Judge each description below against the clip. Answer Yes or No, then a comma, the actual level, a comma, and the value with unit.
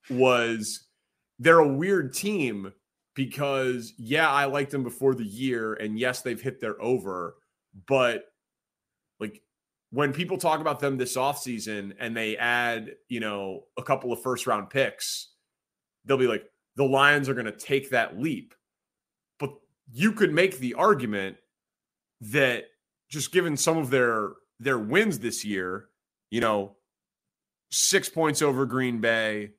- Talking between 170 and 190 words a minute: No, average, 150 wpm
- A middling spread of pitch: Yes, average, 4.2 semitones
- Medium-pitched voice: No, low, 130 Hz